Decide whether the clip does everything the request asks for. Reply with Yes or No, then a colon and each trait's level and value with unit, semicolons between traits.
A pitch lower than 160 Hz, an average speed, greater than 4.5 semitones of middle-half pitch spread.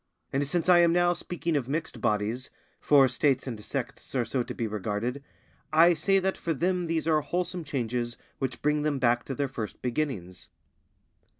Yes: medium, 140 Hz; average, 185 wpm; wide, 5.4 semitones